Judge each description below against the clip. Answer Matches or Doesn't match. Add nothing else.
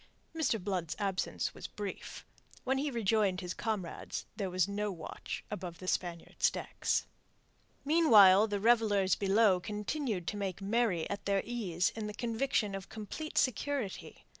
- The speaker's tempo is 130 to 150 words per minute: Matches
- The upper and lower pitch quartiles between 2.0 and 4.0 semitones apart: Matches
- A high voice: Matches